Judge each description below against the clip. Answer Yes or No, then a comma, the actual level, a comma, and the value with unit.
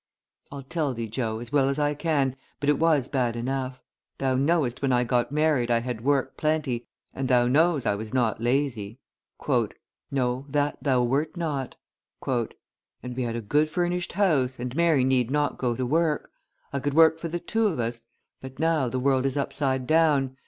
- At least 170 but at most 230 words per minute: Yes, average, 190 wpm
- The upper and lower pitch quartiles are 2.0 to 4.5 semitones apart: Yes, average, 3.5 semitones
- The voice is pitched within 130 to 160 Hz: Yes, low, 135 Hz